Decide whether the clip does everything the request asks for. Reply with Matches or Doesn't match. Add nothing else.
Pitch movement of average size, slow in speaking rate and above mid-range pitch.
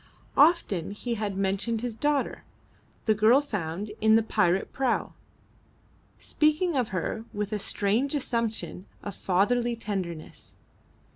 Matches